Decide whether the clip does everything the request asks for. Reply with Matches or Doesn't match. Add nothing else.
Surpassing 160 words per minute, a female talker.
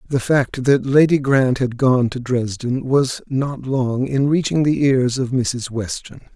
Doesn't match